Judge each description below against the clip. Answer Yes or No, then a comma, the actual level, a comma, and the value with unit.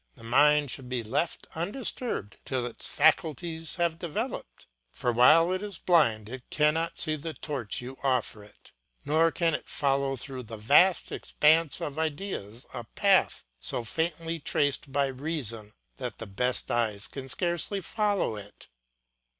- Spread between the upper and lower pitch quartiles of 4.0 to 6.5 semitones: Yes, average, 5.2 semitones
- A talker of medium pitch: Yes, medium, 145 Hz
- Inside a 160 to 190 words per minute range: No, average, 150 wpm